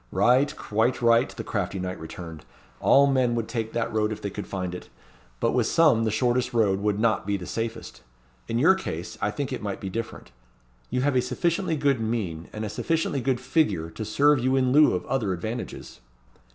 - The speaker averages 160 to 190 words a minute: No, fast, 205 wpm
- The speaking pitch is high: No, low, 115 Hz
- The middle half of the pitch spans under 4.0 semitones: No, average, 4.4 semitones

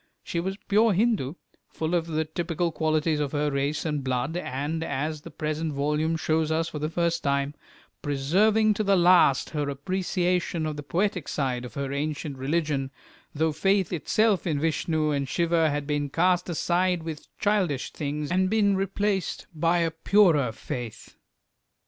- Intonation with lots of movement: No, average, 3.5 semitones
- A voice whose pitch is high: No, medium, 160 Hz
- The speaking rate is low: No, average, 165 wpm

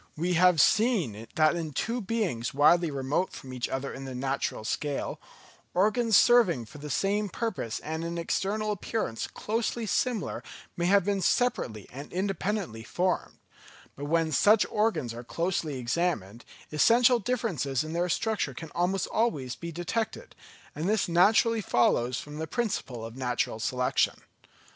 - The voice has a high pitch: No, medium, 170 Hz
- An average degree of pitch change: No, wide, 7.7 semitones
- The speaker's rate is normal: Yes, average, 150 wpm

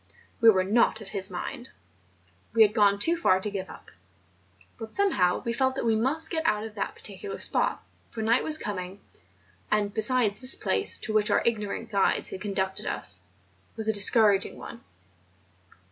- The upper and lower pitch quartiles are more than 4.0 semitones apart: No, average, 2.9 semitones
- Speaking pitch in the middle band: No, high, 215 Hz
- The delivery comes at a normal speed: Yes, average, 180 wpm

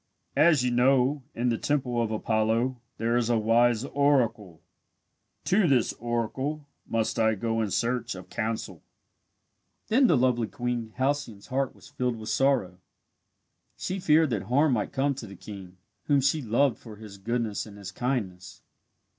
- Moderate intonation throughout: Yes, average, 3.5 semitones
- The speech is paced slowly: No, average, 160 wpm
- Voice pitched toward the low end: Yes, low, 120 Hz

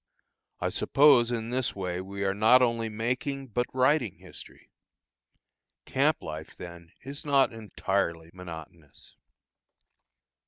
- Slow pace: Yes, slow, 115 wpm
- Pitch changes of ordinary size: No, wide, 5.8 semitones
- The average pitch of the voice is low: Yes, low, 110 Hz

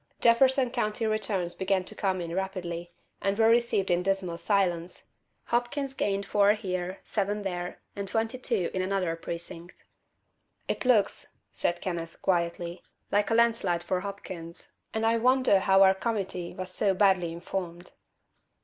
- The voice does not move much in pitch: No, average, 3.5 semitones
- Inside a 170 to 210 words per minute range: No, average, 150 wpm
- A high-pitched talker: Yes, high, 195 Hz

